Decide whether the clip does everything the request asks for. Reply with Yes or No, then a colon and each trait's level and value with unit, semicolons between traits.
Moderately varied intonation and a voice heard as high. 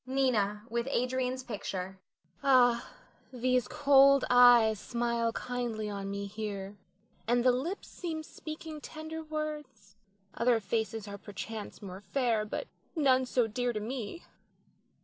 Yes: average, 3.9 semitones; high, 240 Hz